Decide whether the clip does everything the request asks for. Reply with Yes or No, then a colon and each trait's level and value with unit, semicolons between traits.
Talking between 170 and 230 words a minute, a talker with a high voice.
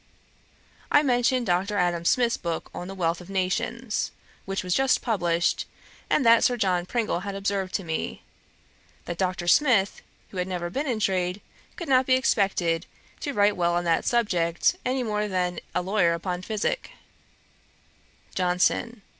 No: average, 160 wpm; high, 195 Hz